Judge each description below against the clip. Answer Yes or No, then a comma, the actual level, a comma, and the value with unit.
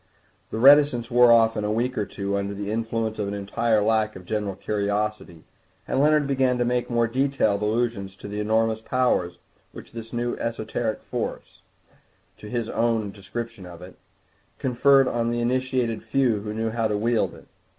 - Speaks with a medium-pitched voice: No, low, 115 Hz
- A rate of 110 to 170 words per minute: No, average, 180 wpm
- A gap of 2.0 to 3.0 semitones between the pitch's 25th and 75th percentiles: Yes, narrow, 2.5 semitones